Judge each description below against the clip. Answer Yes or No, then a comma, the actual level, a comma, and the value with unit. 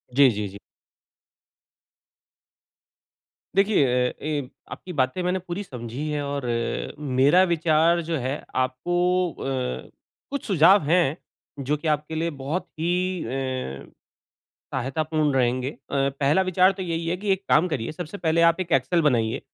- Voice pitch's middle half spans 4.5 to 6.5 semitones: Yes, average, 5.0 semitones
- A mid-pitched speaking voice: Yes, medium, 155 Hz